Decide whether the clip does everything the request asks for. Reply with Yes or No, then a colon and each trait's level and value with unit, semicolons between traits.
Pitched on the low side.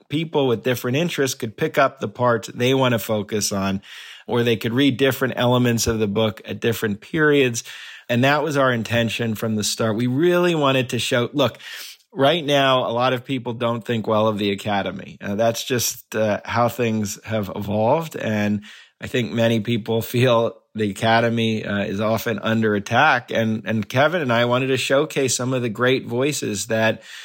Yes: low, 115 Hz